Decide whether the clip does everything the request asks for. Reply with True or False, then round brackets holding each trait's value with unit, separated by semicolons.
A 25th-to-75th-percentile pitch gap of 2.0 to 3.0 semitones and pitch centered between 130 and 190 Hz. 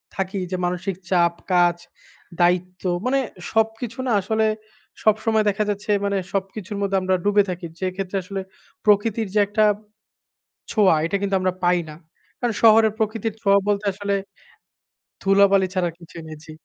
False (2.7 semitones; 200 Hz)